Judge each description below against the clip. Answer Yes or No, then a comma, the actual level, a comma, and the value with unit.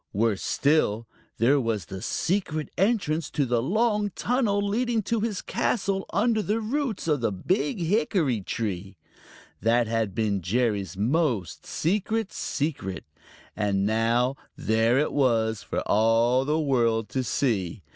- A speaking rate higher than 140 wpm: No, slow, 135 wpm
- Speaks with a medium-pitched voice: No, low, 130 Hz